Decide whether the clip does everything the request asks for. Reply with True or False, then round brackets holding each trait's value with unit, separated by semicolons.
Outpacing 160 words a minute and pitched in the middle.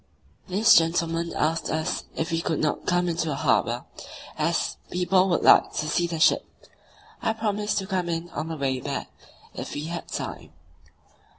True (175 wpm; 170 Hz)